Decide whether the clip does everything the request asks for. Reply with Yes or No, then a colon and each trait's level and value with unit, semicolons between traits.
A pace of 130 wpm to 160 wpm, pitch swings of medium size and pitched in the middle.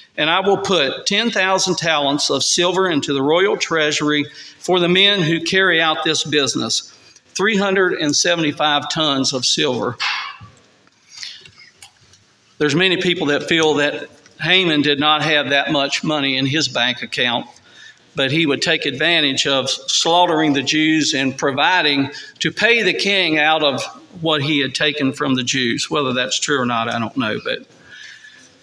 Yes: average, 155 wpm; average, 3.7 semitones; medium, 155 Hz